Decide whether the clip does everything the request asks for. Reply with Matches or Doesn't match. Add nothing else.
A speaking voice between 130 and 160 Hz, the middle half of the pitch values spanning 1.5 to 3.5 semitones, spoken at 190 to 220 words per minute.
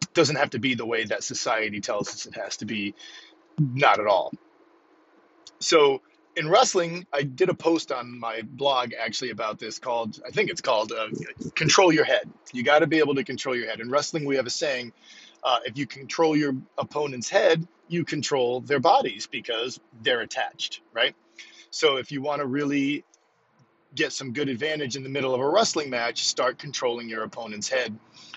Doesn't match